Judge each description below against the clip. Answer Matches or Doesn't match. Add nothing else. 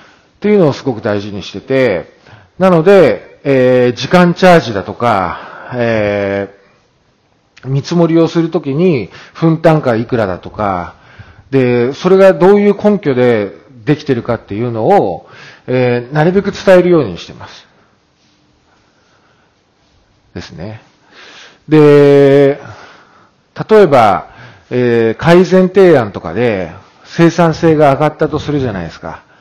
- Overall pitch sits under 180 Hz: Matches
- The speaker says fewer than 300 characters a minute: Matches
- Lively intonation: Matches